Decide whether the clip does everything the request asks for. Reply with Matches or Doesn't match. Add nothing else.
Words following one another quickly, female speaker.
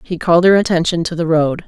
Matches